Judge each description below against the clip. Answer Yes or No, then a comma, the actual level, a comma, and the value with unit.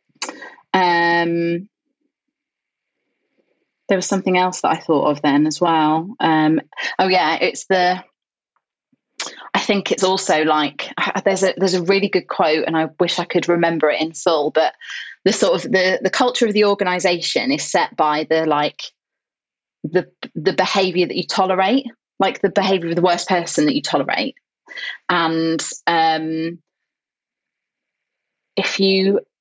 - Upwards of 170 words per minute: No, average, 150 wpm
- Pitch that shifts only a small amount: No, average, 3.3 semitones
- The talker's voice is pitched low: No, medium, 185 Hz